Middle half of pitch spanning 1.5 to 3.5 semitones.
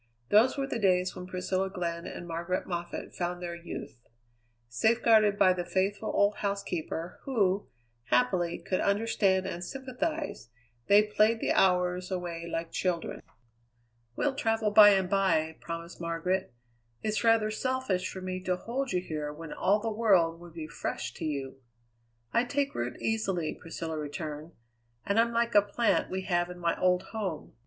No: average, 3.9 semitones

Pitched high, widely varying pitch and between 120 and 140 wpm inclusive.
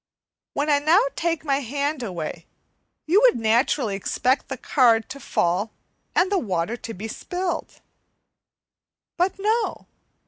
Yes: very high, 275 Hz; wide, 7.3 semitones; slow, 135 wpm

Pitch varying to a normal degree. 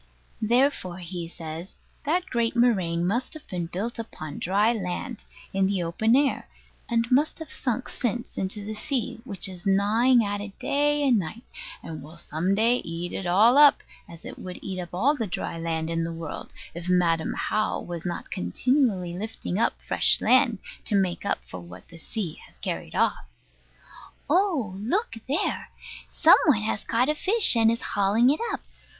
No: wide, 5.8 semitones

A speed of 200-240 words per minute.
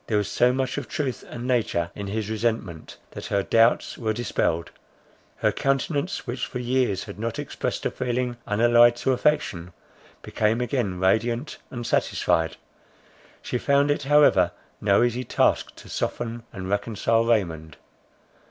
No: average, 150 wpm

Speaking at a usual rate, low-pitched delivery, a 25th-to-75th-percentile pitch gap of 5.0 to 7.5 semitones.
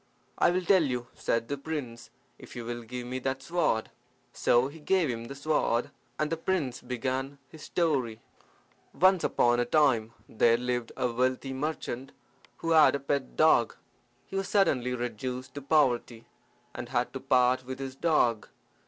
No: average, 170 wpm; low, 130 Hz; average, 4.1 semitones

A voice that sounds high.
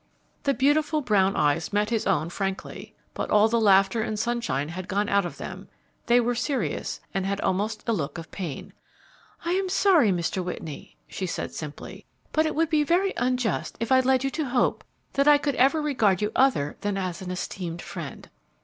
Yes: high, 215 Hz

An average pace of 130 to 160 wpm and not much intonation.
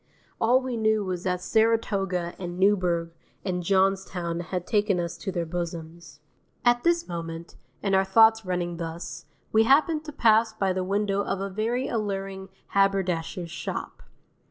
No: average, 155 wpm; average, 3.8 semitones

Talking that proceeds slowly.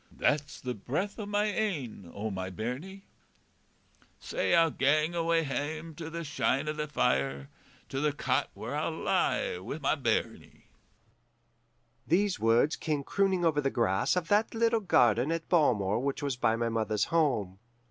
No: average, 160 wpm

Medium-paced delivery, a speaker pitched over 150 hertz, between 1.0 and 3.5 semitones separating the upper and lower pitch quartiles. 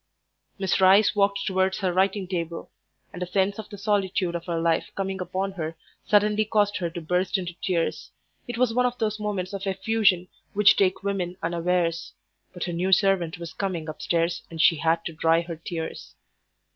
Yes: average, 185 wpm; medium, 185 Hz; average, 2.7 semitones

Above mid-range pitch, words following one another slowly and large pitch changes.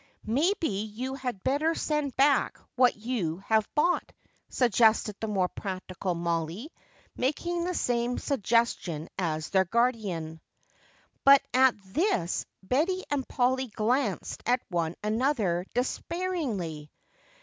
Yes: high, 235 Hz; slow, 115 wpm; wide, 6.6 semitones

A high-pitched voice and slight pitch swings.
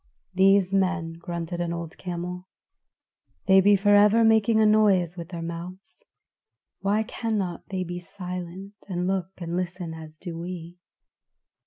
No: medium, 180 Hz; narrow, 2.3 semitones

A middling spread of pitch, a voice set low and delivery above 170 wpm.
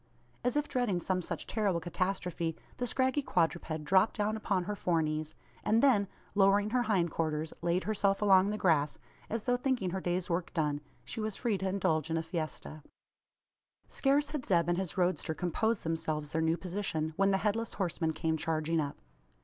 No: average, 4.4 semitones; medium, 185 Hz; average, 185 wpm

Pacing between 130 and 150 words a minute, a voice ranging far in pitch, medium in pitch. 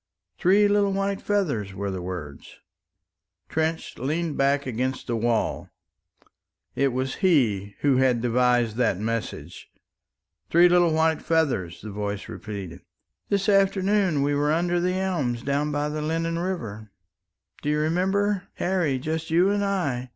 Yes: average, 145 wpm; wide, 6.9 semitones; medium, 150 Hz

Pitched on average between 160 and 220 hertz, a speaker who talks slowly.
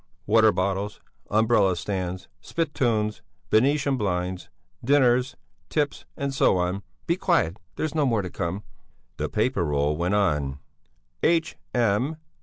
No: low, 105 Hz; slow, 115 wpm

